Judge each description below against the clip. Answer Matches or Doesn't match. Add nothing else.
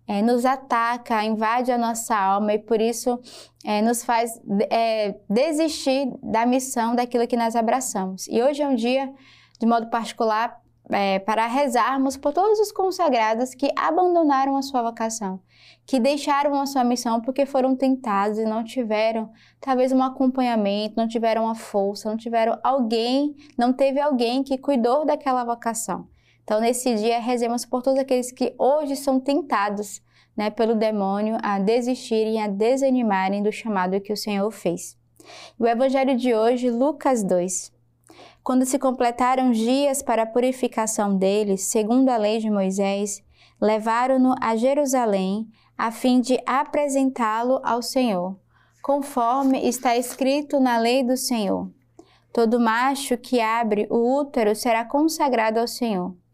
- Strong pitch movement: Doesn't match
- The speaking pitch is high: Matches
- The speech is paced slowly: Doesn't match